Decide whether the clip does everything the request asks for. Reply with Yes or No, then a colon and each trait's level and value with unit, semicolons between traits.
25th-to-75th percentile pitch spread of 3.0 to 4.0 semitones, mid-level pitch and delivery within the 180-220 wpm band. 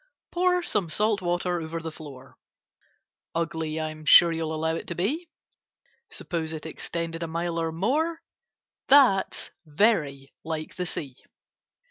No: average, 3.5 semitones; medium, 165 Hz; slow, 135 wpm